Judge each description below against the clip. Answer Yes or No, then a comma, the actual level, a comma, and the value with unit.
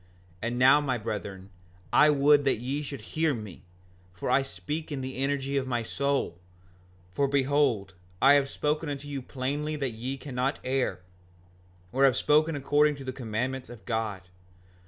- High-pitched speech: No, low, 135 Hz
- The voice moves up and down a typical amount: Yes, average, 3.0 semitones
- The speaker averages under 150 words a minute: No, average, 170 wpm